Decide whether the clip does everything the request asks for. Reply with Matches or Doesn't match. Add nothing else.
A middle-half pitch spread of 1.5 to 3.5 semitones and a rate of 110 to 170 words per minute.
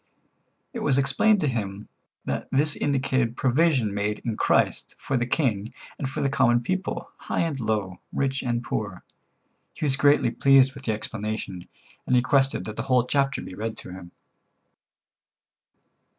Doesn't match